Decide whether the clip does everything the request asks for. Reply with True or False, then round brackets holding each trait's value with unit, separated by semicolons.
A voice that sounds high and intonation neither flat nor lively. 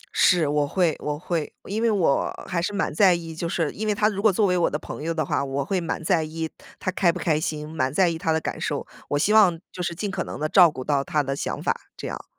False (165 Hz; 3.7 semitones)